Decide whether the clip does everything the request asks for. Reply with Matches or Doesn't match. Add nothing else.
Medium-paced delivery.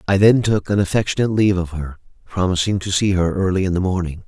Doesn't match